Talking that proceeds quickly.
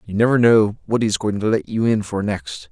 Yes: fast, 265 wpm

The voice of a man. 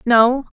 No: female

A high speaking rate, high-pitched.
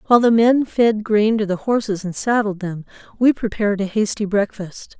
No: average, 190 wpm; high, 210 Hz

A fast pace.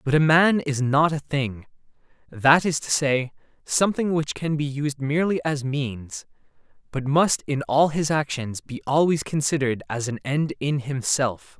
No: average, 170 wpm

